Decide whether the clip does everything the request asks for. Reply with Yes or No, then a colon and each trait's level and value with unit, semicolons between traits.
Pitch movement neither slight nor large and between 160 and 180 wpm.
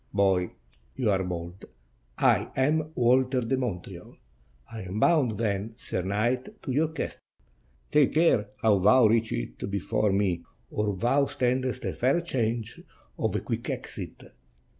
No: average, 4.7 semitones; average, 145 wpm